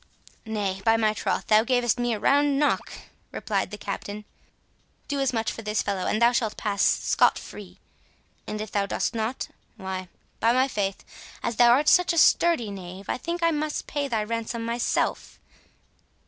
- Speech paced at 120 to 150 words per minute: No, average, 175 wpm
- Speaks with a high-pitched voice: Yes, high, 225 Hz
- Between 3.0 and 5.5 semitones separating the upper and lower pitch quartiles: Yes, average, 3.8 semitones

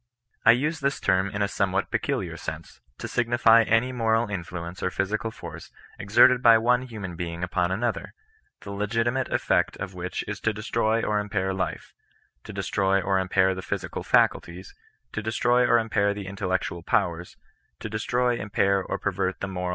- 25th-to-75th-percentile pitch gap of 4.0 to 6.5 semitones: No, average, 3.4 semitones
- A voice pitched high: No, low, 100 Hz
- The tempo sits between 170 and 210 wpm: Yes, average, 180 wpm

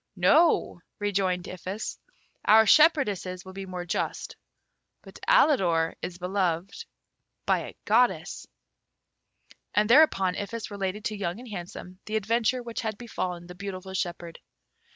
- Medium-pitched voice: No, high, 195 Hz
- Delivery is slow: Yes, slow, 130 wpm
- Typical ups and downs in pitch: Yes, average, 3.6 semitones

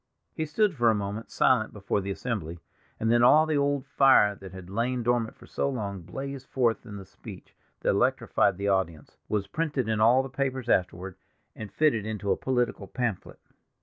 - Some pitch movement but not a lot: Yes, average, 4.9 semitones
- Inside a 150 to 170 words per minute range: No, average, 190 wpm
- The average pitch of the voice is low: Yes, low, 115 Hz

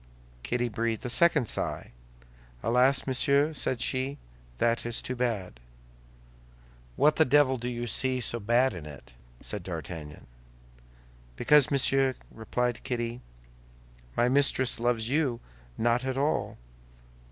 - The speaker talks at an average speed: No, slow, 125 wpm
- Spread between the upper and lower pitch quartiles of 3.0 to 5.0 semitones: No, narrow, 2.4 semitones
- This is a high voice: No, low, 125 Hz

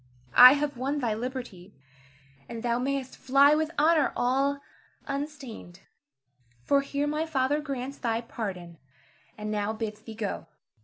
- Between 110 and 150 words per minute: Yes, average, 140 wpm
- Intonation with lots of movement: No, average, 4.3 semitones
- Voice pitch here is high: Yes, very high, 260 Hz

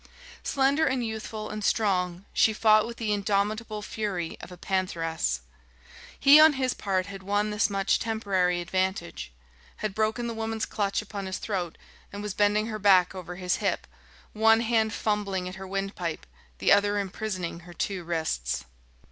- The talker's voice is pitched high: Yes, high, 200 Hz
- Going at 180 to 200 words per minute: No, average, 165 wpm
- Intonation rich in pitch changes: No, average, 2.9 semitones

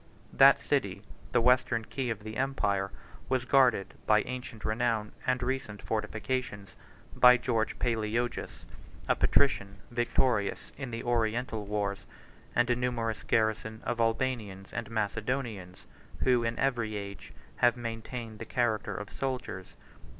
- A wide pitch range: No, narrow, 2.6 semitones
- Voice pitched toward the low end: Yes, low, 115 Hz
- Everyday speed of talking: No, slow, 130 wpm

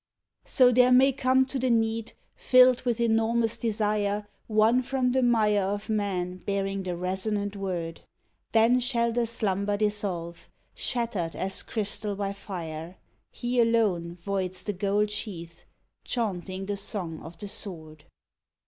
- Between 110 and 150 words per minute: Yes, average, 140 wpm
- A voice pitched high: Yes, high, 205 Hz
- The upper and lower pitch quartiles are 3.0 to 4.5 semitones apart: Yes, average, 3.7 semitones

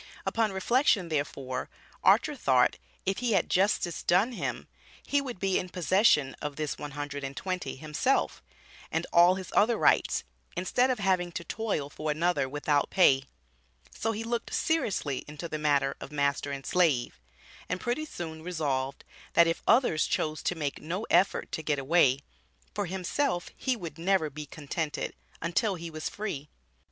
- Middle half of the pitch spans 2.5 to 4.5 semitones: No, average, 4.9 semitones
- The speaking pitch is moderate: Yes, medium, 170 Hz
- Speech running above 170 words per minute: No, average, 165 wpm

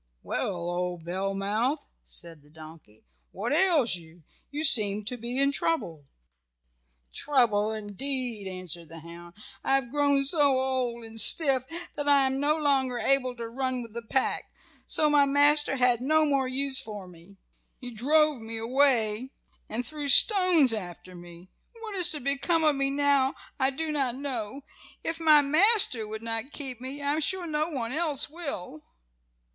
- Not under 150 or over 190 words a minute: Yes, average, 165 wpm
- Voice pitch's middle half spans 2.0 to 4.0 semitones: No, average, 5.3 semitones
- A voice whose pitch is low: No, very high, 260 Hz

